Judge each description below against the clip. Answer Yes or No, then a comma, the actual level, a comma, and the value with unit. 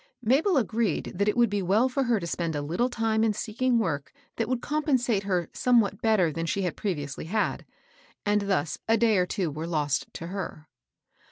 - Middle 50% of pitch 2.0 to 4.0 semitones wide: No, wide, 5.4 semitones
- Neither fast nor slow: No, fast, 215 wpm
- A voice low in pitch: No, high, 205 Hz